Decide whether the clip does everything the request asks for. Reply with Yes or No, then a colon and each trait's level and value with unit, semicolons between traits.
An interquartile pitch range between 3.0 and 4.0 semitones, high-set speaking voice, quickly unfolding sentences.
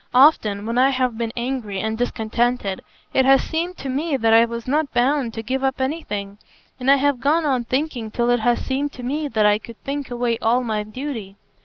Yes: average, 3.4 semitones; high, 245 Hz; fast, 215 wpm